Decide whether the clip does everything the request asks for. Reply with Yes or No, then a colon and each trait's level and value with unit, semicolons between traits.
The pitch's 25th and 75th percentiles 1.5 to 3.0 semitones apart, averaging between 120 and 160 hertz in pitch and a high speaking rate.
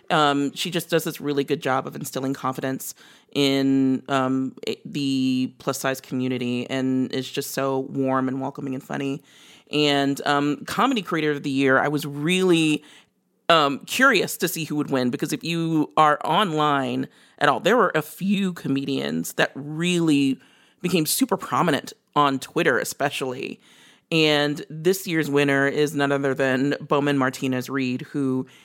No: narrow, 2.6 semitones; medium, 140 Hz; average, 155 wpm